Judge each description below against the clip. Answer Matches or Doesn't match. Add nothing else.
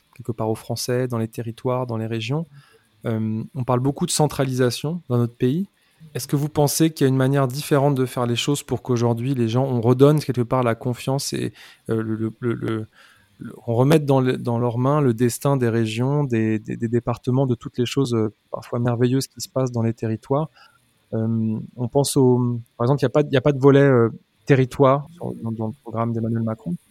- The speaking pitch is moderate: Doesn't match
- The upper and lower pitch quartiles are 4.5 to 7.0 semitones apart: Doesn't match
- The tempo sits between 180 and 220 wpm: Matches